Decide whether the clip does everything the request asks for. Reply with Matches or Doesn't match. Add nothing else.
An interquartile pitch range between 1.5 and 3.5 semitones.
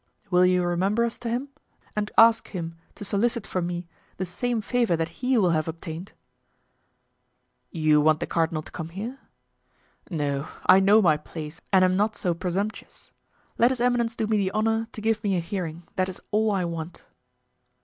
Doesn't match